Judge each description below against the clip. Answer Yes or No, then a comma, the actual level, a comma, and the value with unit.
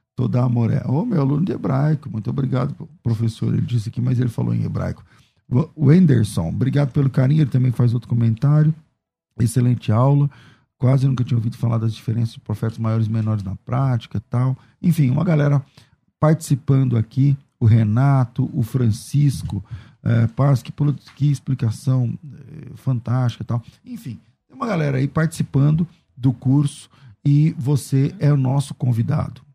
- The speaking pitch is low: Yes, low, 130 Hz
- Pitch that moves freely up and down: No, average, 3.4 semitones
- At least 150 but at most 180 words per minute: Yes, average, 155 wpm